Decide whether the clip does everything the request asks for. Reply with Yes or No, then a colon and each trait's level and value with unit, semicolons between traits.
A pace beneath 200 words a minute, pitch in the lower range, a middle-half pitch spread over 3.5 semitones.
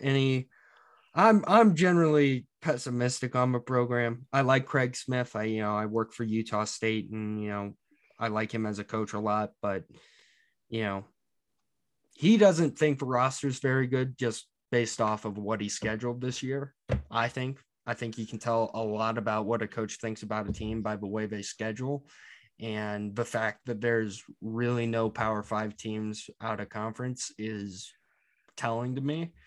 No: average, 185 wpm; low, 115 Hz; average, 3.1 semitones